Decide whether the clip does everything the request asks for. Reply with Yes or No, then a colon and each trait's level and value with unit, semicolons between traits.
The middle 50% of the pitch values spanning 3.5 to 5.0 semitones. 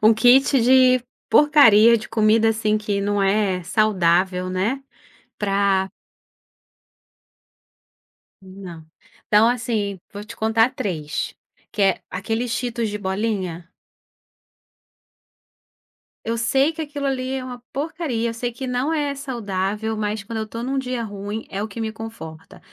Yes: average, 3.9 semitones